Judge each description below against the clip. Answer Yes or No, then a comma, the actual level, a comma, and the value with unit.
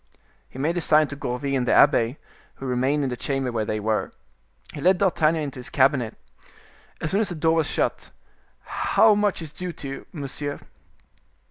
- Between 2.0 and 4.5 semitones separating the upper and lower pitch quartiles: Yes, average, 4.0 semitones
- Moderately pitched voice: Yes, medium, 145 Hz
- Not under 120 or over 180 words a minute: No, average, 190 wpm